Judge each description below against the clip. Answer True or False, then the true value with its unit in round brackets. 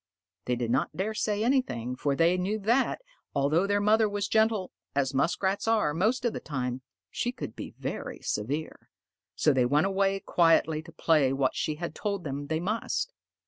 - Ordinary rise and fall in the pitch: False (6.9 semitones)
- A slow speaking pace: False (185 wpm)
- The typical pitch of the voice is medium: True (175 Hz)